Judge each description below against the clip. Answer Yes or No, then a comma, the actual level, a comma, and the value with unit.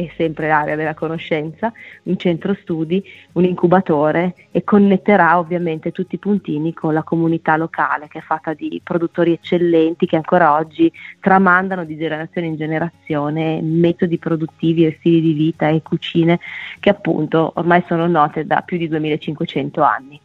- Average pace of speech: Yes, average, 155 wpm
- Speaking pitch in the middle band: Yes, medium, 165 Hz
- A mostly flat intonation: Yes, narrow, 1.9 semitones